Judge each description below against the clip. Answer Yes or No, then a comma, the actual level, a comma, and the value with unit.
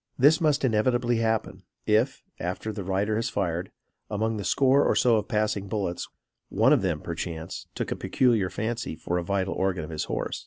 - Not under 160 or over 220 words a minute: Yes, average, 190 wpm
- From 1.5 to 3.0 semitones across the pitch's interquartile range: No, average, 3.8 semitones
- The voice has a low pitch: Yes, low, 105 Hz